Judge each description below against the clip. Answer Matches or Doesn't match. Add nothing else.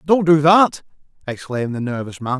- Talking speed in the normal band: Matches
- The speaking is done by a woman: Doesn't match